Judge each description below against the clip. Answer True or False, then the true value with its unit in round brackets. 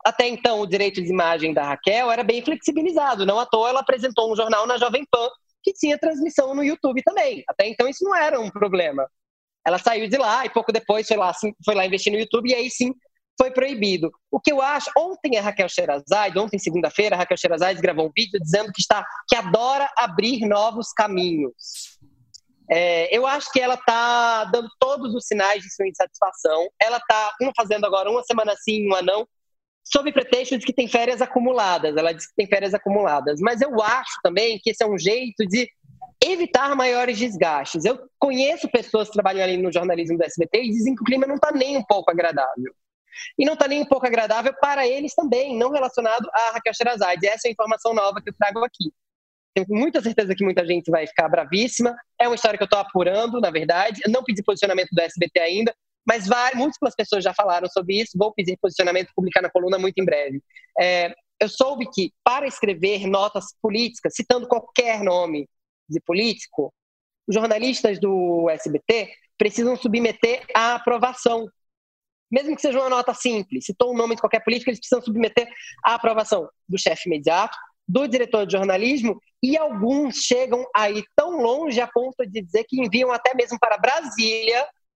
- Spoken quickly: True (195 wpm)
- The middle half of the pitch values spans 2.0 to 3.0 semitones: False (4.5 semitones)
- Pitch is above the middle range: True (225 Hz)